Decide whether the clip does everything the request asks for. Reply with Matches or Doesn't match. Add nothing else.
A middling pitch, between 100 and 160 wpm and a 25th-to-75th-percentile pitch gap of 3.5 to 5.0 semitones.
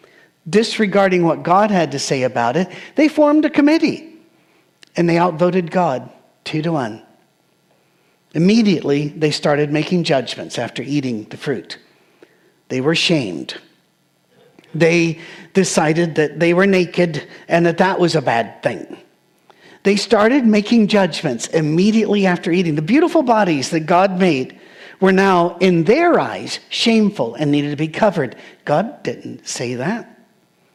Matches